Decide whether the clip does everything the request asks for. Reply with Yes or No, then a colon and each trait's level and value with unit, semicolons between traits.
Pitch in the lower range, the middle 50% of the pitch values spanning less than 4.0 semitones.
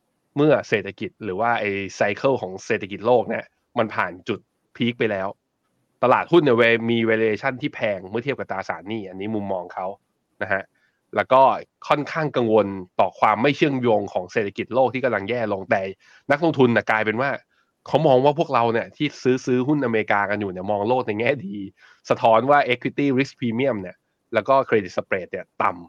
No: low, 115 Hz; average, 4.6 semitones